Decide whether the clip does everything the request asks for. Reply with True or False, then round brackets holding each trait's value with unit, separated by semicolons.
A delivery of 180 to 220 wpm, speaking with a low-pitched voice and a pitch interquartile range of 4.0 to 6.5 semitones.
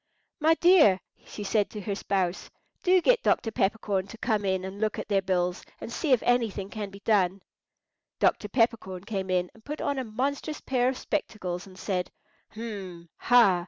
False (185 wpm; 210 Hz; 4.4 semitones)